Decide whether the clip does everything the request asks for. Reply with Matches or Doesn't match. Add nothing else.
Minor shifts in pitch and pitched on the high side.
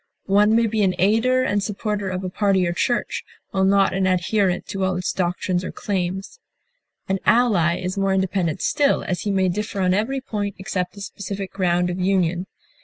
Matches